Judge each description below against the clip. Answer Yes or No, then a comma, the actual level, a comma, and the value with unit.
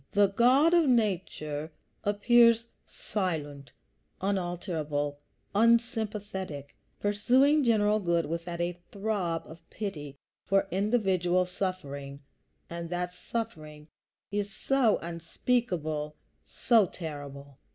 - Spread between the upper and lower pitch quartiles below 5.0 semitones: No, wide, 5.4 semitones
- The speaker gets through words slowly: Yes, slow, 90 wpm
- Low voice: No, medium, 185 Hz